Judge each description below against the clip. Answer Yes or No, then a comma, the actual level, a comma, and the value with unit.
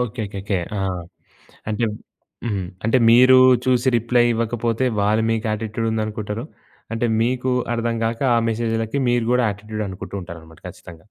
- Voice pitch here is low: Yes, low, 115 Hz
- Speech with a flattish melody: Yes, narrow, 2.1 semitones